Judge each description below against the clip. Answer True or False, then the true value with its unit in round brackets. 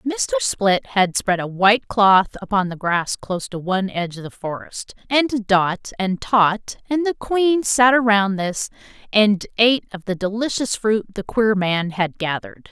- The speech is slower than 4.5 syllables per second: True (4.3 syllables/s)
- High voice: True (210 Hz)